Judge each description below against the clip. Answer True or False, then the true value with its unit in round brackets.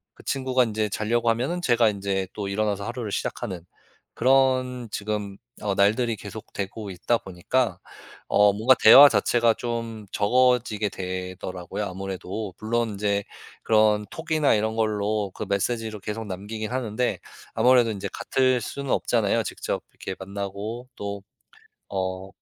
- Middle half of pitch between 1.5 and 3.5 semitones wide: True (3.1 semitones)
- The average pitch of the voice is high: False (110 Hz)